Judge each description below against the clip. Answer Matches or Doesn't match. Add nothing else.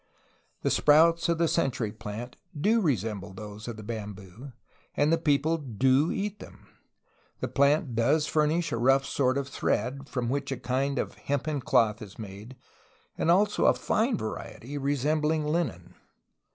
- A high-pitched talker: Doesn't match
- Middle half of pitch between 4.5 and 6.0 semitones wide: Matches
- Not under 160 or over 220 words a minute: Matches